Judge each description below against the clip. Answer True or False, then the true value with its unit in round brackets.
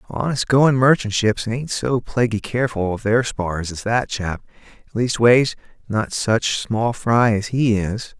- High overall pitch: False (115 Hz)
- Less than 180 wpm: True (155 wpm)